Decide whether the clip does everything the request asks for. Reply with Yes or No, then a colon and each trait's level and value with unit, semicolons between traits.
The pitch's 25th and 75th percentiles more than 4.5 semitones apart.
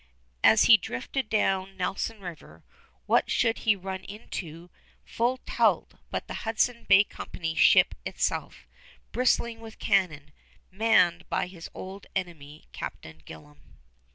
Yes: average, 5.0 semitones